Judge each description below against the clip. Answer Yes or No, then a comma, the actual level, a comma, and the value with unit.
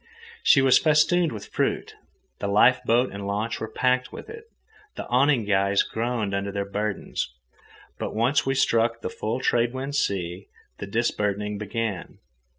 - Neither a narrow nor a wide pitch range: Yes, average, 4.2 semitones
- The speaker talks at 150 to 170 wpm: Yes, average, 155 wpm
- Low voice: Yes, low, 115 Hz